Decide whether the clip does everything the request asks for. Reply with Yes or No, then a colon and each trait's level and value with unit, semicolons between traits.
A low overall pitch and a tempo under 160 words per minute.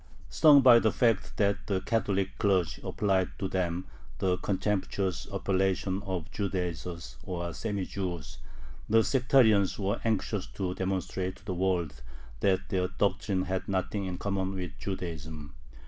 Yes: very low, 95 Hz; average, 140 wpm